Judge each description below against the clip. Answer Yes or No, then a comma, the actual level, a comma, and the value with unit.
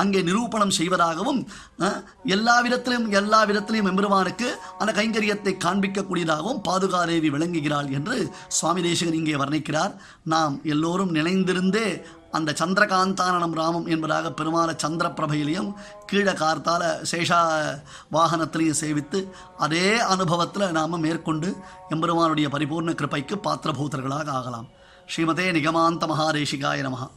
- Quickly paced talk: No, average, 100 wpm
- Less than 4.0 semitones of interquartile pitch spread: Yes, average, 3.4 semitones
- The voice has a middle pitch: Yes, medium, 170 Hz